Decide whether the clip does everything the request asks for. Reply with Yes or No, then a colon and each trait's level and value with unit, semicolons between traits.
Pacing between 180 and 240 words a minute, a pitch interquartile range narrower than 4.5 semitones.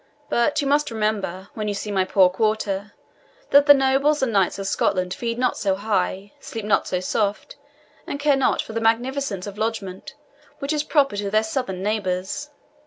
No: average, 185 wpm; average, 5.3 semitones